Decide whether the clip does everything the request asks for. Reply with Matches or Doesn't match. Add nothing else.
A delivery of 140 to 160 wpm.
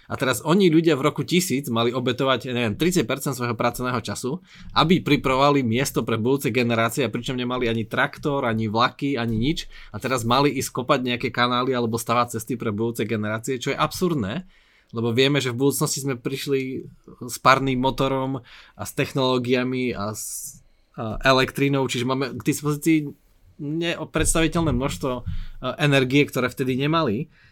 Matches